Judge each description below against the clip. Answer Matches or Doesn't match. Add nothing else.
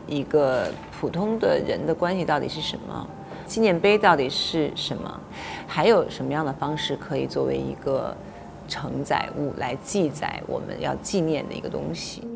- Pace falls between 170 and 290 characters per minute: Matches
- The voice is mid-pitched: Matches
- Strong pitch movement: Matches